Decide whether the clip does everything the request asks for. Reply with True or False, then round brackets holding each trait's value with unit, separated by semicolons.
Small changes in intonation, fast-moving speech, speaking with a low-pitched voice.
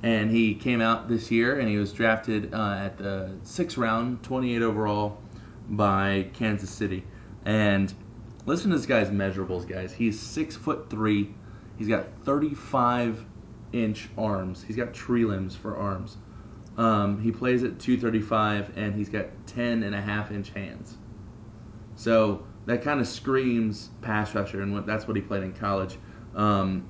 False (2.1 semitones; 160 wpm; 110 Hz)